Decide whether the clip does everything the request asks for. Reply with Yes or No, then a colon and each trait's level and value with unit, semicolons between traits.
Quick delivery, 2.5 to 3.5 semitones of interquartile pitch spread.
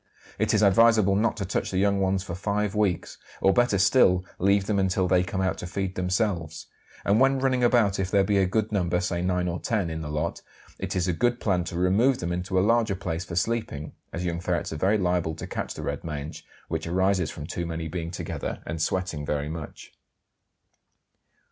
Yes: fast, 215 wpm; average, 2.9 semitones